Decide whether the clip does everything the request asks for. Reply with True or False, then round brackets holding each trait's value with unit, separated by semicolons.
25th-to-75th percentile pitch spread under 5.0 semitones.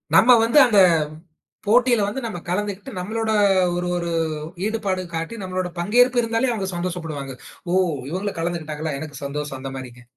False (5.6 semitones)